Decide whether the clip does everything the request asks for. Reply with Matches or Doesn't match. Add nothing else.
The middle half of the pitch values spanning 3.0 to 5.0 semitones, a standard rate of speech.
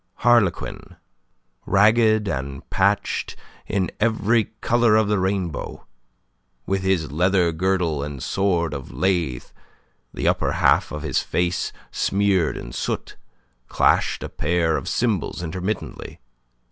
Doesn't match